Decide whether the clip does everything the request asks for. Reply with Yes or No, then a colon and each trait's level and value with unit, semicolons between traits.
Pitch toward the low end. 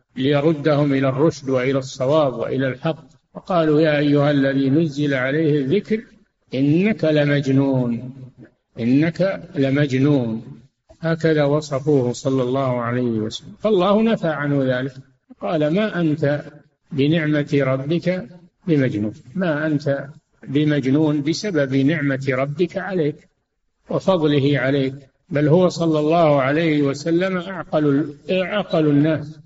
No: medium, 145 Hz